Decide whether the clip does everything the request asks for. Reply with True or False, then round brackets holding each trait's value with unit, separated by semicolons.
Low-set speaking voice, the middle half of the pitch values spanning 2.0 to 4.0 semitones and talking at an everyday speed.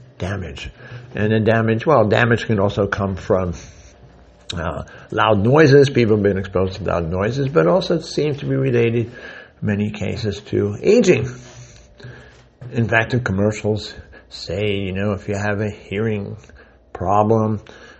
True (110 Hz; 2.9 semitones; 145 wpm)